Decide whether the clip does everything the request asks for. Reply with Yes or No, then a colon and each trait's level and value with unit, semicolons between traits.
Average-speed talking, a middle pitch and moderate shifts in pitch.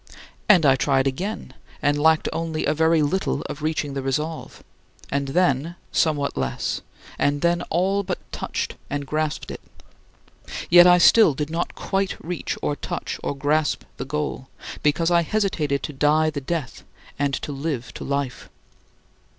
Yes: average, 160 wpm; medium, 150 Hz; average, 3.1 semitones